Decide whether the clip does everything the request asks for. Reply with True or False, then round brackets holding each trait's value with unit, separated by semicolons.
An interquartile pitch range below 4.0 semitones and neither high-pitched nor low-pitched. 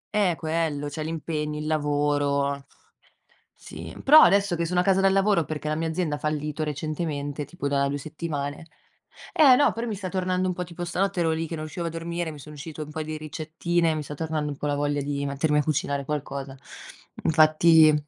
True (2.7 semitones; 155 Hz)